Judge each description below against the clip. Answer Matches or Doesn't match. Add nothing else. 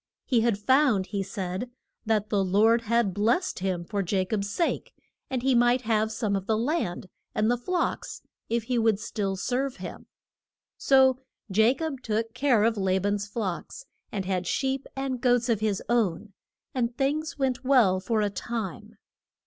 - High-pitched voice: Matches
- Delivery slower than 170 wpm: Doesn't match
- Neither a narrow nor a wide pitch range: Matches